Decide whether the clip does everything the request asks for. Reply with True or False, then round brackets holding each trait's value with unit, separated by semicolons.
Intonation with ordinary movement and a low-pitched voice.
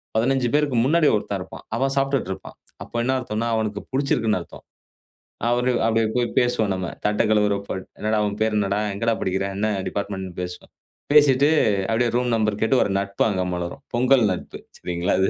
True (3.9 semitones; 110 Hz)